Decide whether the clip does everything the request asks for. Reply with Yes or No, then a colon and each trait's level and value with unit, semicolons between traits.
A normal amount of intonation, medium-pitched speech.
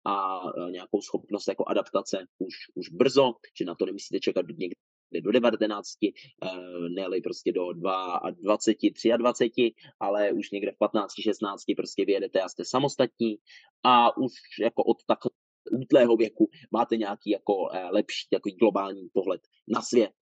No: average, 3.2 semitones; low, 110 Hz